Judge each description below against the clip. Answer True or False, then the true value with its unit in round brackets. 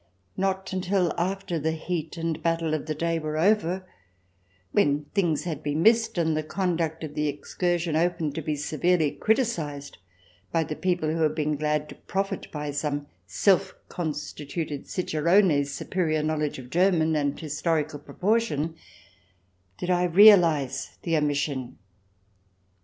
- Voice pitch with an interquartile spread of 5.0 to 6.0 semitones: False (3.1 semitones)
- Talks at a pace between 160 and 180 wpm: False (145 wpm)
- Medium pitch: True (160 Hz)